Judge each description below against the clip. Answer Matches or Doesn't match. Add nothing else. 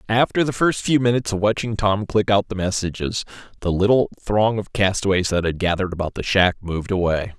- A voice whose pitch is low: Matches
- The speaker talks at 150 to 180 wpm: Doesn't match